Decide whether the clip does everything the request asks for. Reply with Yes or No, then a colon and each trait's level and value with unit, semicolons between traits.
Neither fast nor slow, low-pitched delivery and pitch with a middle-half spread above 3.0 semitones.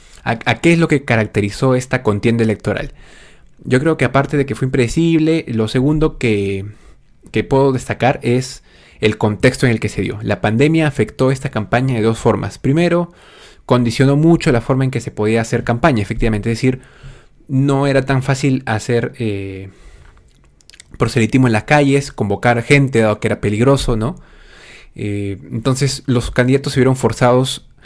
Yes: average, 165 wpm; low, 125 Hz; average, 4.0 semitones